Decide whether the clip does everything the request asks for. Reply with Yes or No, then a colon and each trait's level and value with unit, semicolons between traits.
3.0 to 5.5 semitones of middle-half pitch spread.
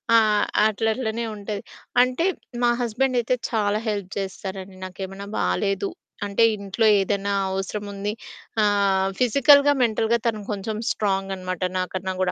No: narrow, 2.6 semitones